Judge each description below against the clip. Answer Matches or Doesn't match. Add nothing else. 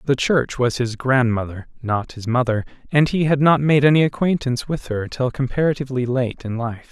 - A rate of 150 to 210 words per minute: Matches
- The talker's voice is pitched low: Matches